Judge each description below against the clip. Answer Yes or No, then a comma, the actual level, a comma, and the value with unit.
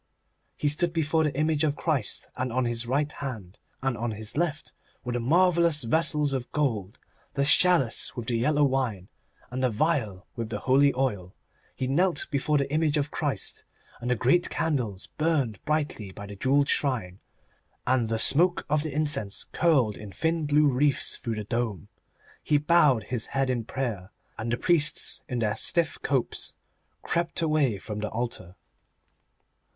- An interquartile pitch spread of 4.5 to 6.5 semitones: Yes, average, 5.0 semitones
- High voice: No, low, 135 Hz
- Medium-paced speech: Yes, average, 170 wpm